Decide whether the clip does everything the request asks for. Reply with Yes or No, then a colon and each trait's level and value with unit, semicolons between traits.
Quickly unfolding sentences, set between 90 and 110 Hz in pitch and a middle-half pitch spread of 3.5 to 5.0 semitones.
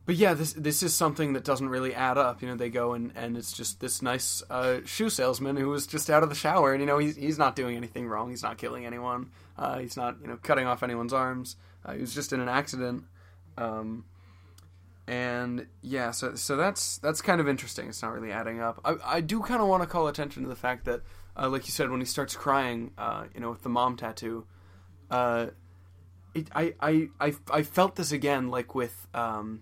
No: fast, 235 wpm; low, 125 Hz; average, 4.3 semitones